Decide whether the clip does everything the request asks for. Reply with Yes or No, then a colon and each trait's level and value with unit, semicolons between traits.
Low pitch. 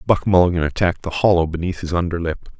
Yes: very low, 85 Hz